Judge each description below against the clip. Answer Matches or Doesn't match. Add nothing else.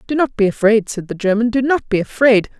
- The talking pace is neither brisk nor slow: Doesn't match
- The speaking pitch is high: Matches